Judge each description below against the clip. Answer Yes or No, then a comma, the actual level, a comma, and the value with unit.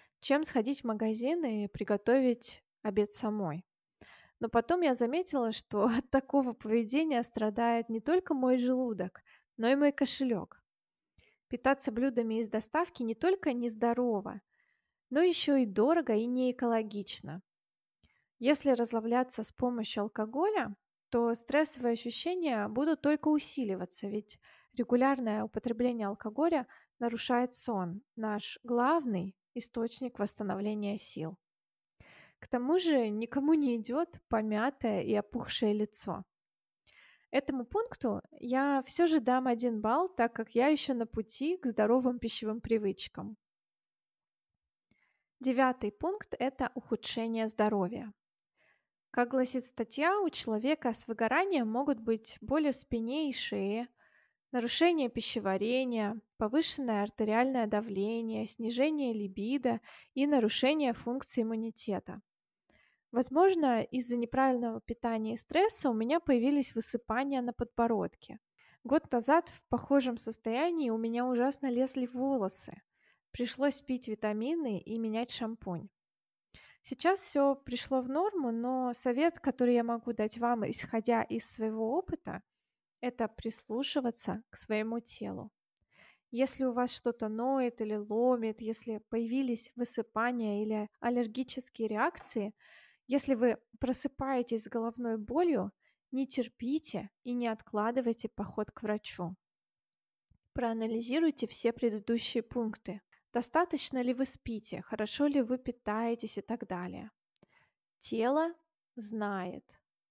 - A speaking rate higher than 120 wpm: No, average, 115 wpm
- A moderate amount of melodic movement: Yes, average, 3.3 semitones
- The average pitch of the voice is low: No, high, 240 Hz